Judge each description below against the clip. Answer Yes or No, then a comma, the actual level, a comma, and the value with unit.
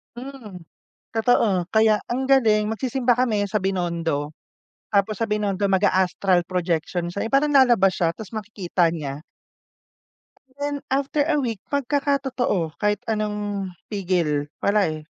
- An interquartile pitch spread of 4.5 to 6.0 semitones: Yes, average, 5.2 semitones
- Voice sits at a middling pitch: No, high, 210 Hz